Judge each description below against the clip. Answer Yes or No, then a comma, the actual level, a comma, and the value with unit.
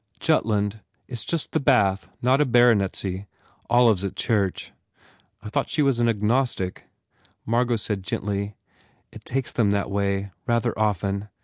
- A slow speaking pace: No, average, 145 wpm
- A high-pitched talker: No, low, 105 Hz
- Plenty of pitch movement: No, average, 3.3 semitones